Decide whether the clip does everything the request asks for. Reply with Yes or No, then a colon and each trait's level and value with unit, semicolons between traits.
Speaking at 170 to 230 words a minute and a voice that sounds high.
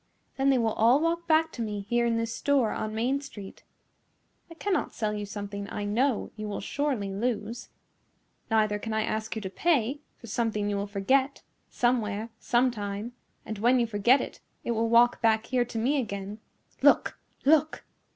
Yes: average, 185 wpm; high, 230 Hz